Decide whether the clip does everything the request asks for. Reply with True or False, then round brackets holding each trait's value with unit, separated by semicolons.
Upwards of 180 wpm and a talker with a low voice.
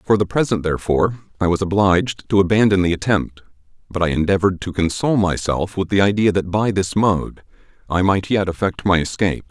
True (190 wpm; 95 Hz)